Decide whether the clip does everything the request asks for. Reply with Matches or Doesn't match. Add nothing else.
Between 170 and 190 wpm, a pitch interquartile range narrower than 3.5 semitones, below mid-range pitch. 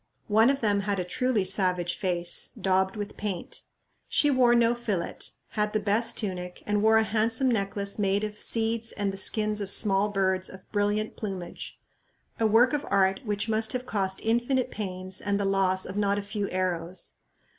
Doesn't match